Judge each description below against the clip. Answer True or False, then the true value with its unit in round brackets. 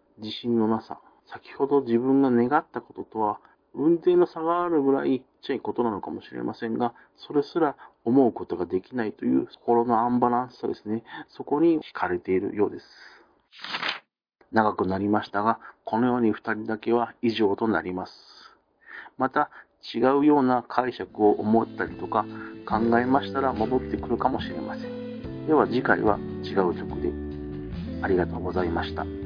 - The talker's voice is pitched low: True (115 Hz)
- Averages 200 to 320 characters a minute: False (335 characters per minute)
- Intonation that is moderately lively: True (4.5 semitones)